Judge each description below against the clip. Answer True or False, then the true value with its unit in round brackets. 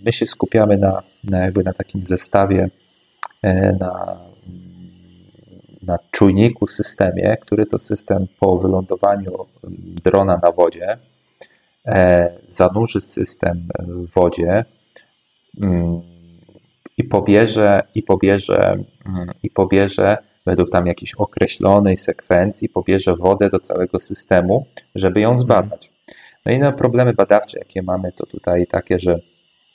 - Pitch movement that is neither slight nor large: False (2.1 semitones)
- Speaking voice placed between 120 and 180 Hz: False (95 Hz)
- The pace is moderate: True (120 wpm)